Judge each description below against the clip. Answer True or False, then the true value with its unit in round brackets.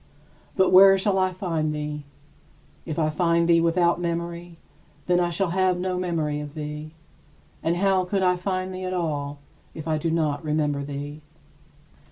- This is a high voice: False (170 Hz)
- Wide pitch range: False (3.1 semitones)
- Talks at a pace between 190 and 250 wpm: False (170 wpm)